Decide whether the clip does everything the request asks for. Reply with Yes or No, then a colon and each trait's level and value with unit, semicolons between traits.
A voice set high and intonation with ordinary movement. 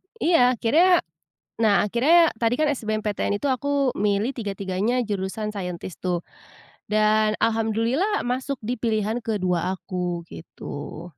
Yes: high, 220 Hz; average, 4.0 semitones